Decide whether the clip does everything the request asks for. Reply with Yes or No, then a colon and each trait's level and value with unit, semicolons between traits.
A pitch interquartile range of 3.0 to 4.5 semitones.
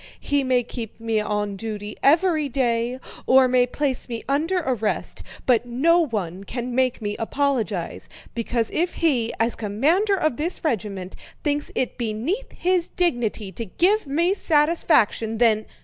No: wide, 5.4 semitones